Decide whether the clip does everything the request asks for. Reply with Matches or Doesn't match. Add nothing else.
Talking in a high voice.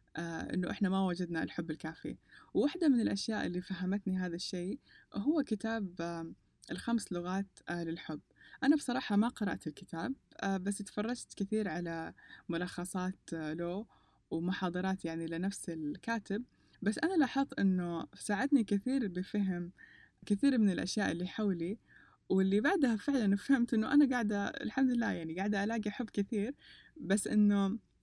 Matches